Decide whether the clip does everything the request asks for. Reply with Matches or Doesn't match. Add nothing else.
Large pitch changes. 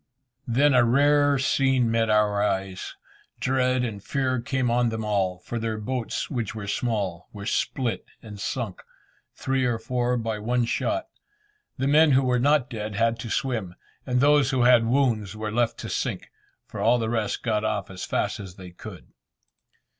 Doesn't match